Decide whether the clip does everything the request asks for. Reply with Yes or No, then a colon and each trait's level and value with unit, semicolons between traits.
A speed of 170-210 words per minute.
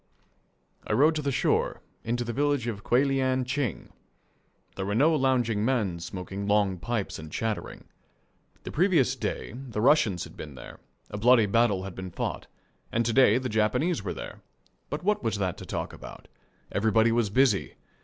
Yes: average, 175 wpm